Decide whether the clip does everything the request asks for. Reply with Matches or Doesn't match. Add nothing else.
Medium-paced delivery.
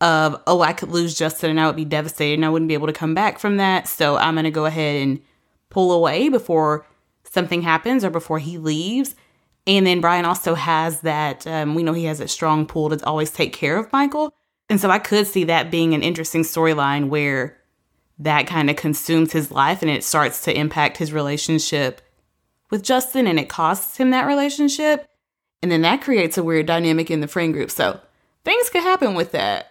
Doesn't match